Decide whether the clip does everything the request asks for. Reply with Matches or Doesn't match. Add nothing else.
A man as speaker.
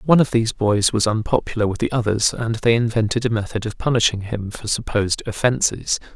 Matches